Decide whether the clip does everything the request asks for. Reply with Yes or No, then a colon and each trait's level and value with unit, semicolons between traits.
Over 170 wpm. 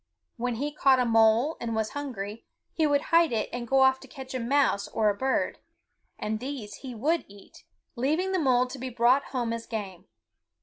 Yes: fast, 205 wpm